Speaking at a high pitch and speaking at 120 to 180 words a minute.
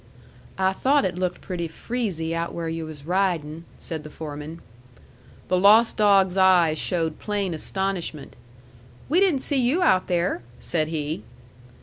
No: medium, 180 Hz; average, 145 wpm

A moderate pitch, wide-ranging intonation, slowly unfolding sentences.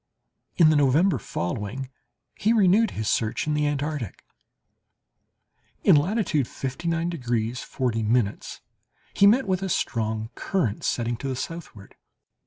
Yes: medium, 145 Hz; wide, 6.8 semitones; slow, 125 wpm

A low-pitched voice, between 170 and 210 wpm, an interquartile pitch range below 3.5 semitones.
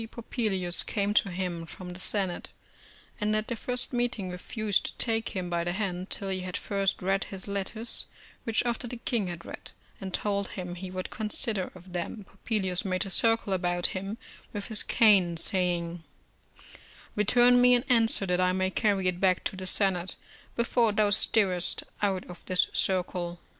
No: high, 195 Hz; average, 180 wpm; average, 3.1 semitones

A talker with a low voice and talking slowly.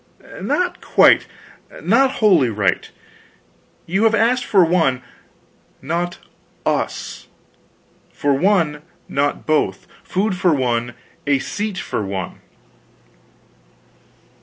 No: medium, 170 Hz; slow, 95 wpm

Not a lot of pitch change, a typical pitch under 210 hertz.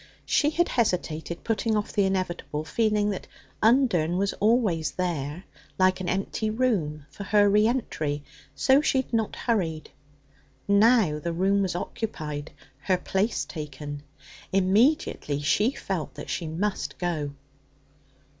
No: wide, 5.4 semitones; high, 190 Hz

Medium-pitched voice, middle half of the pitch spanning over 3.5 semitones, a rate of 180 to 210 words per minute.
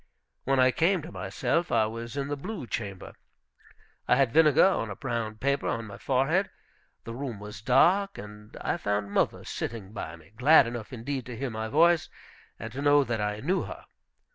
No: low, 125 Hz; average, 5.0 semitones; average, 190 wpm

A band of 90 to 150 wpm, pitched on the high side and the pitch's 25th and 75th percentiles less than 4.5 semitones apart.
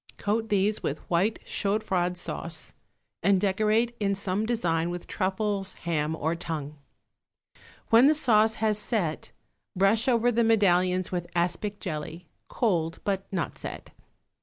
Yes: slow, 135 wpm; high, 195 Hz; average, 3.9 semitones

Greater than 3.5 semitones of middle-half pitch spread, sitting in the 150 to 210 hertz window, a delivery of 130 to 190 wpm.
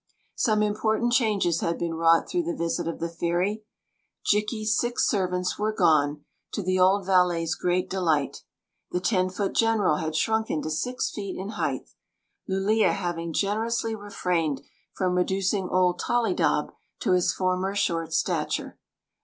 Yes: average, 3.9 semitones; medium, 185 Hz; average, 155 wpm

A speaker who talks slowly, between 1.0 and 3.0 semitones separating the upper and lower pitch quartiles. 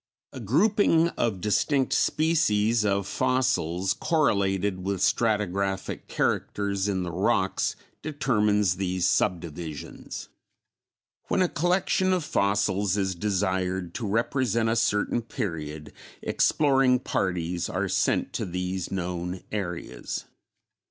No: slow, 105 wpm; average, 5.2 semitones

